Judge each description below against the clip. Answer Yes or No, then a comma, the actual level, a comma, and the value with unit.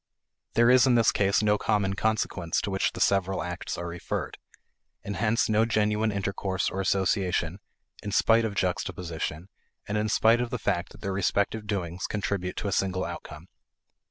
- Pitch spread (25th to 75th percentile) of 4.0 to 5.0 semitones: No, narrow, 2.6 semitones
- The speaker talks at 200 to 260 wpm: No, average, 175 wpm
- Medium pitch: No, low, 100 Hz